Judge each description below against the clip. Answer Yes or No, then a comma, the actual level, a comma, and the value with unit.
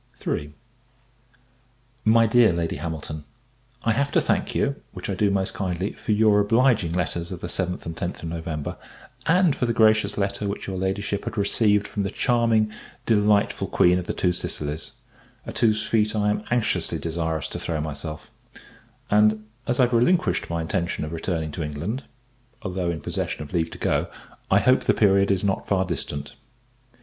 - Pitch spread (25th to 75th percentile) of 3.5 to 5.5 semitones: Yes, average, 4.3 semitones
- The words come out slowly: No, average, 180 wpm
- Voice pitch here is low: Yes, low, 100 Hz